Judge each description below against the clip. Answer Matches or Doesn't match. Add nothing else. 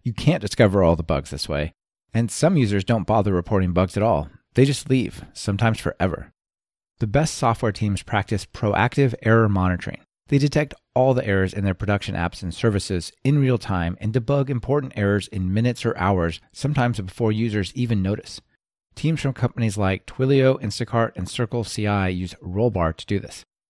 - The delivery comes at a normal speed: Matches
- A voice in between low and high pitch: Doesn't match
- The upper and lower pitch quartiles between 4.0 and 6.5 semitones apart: Matches